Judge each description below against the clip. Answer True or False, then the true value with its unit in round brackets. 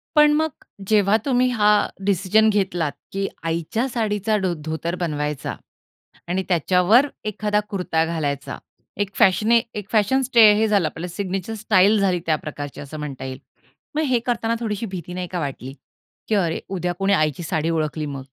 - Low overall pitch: False (190 Hz)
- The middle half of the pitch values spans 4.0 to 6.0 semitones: True (4.9 semitones)